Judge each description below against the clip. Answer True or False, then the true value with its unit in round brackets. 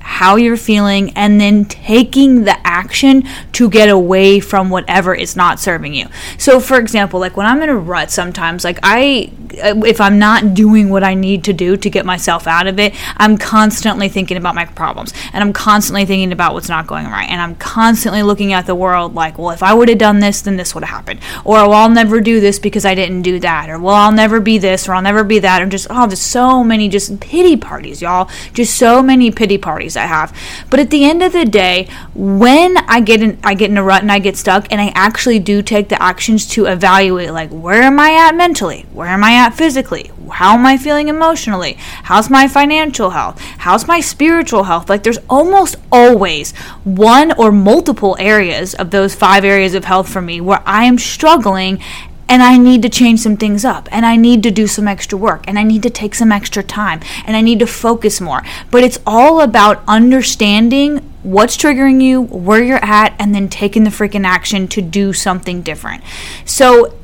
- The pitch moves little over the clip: False (3.7 semitones)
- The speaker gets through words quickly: True (220 wpm)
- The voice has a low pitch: False (210 Hz)